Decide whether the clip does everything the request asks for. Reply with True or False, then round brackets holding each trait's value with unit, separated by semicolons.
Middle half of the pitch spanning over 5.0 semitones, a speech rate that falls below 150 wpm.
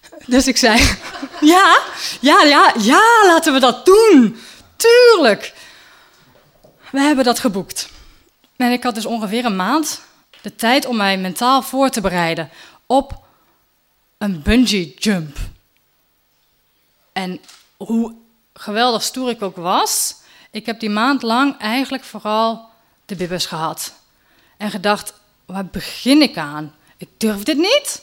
True (5.6 semitones; 135 wpm)